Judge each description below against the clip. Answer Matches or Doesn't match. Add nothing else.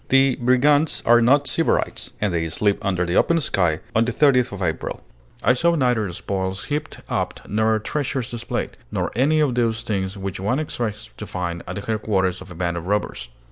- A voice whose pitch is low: Matches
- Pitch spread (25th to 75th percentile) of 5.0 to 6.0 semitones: Matches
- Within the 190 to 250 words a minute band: Matches